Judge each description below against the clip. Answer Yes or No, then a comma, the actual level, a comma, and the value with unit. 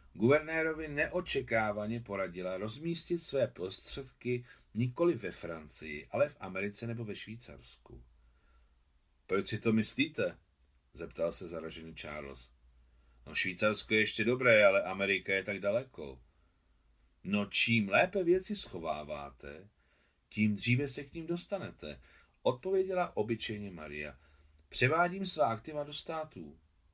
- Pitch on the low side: Yes, low, 105 Hz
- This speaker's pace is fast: No, slow, 115 wpm